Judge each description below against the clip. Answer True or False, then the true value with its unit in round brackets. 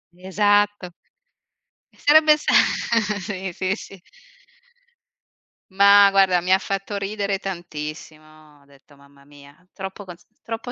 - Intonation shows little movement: False (4.6 semitones)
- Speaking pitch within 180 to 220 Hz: True (190 Hz)